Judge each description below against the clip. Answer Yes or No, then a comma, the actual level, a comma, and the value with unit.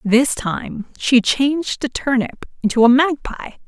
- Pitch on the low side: No, very high, 255 Hz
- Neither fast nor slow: Yes, average, 145 wpm